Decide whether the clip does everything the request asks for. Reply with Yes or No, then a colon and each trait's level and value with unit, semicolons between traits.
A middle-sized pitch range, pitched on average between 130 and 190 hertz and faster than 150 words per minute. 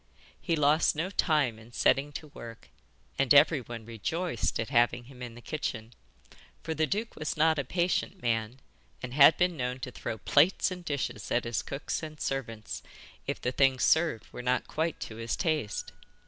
Yes: average, 4.9 semitones; low, 135 Hz; average, 180 wpm